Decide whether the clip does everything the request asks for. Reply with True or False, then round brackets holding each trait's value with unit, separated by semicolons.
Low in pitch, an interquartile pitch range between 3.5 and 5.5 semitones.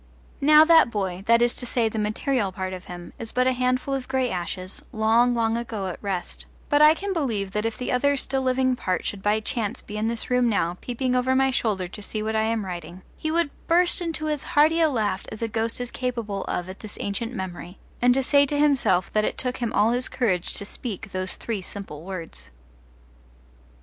False (230 Hz; 4.5 semitones)